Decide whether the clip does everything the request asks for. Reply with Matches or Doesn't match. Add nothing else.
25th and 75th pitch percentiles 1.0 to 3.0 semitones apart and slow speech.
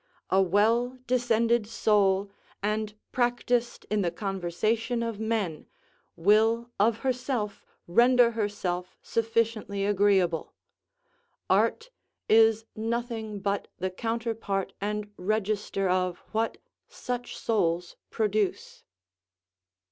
Matches